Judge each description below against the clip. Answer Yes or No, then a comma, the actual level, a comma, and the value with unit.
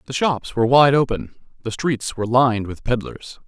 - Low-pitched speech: Yes, low, 125 Hz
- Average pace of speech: Yes, average, 190 wpm